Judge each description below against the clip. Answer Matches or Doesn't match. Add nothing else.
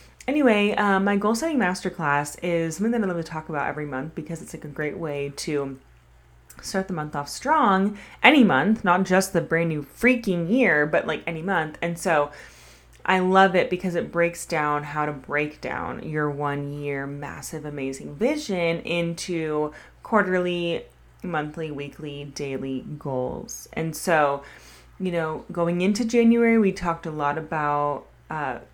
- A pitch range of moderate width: Matches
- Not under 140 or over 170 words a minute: Matches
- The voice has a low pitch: Doesn't match